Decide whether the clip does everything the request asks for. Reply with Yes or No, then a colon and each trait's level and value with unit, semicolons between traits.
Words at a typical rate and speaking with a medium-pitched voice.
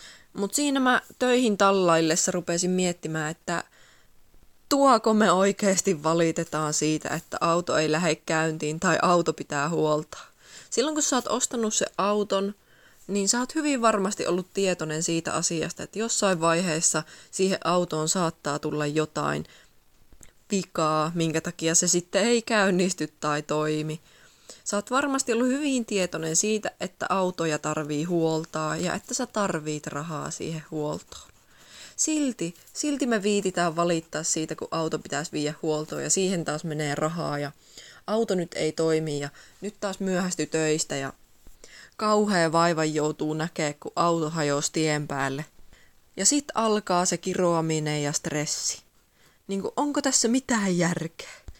Yes: average, 140 wpm; medium, 170 Hz